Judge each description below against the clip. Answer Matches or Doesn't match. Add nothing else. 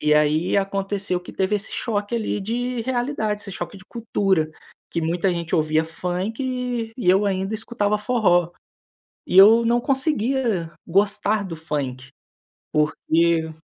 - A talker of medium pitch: Doesn't match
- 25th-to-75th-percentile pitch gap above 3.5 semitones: Matches